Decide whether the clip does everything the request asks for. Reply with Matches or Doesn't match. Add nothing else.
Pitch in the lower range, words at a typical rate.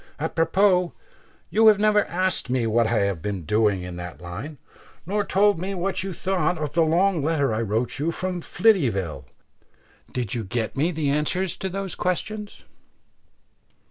Doesn't match